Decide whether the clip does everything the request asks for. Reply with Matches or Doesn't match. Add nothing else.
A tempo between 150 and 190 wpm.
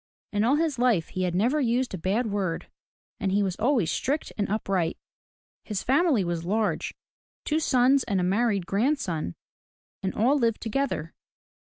Matches